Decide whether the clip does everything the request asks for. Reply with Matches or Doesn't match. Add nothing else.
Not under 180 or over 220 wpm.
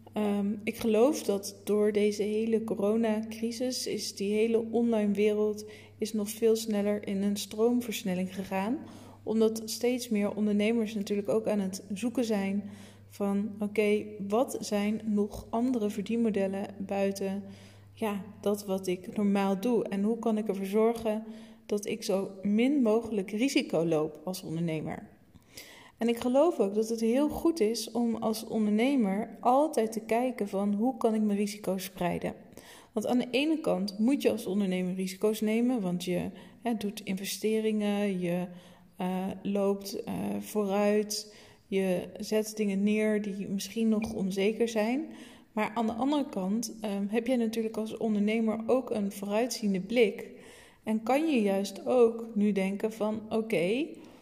Doesn't match